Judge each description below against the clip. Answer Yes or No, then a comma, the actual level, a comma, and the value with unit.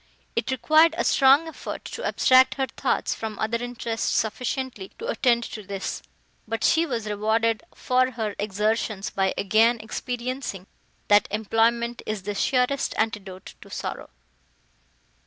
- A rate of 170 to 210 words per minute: No, average, 140 wpm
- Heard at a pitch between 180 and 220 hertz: No, high, 230 Hz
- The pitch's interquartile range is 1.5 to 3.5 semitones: Yes, average, 3.2 semitones